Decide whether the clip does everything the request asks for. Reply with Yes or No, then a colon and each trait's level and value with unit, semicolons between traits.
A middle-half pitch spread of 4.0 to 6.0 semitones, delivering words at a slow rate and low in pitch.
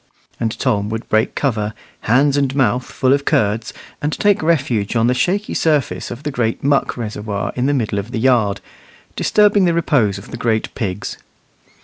No: average, 4.7 semitones; average, 180 wpm; low, 125 Hz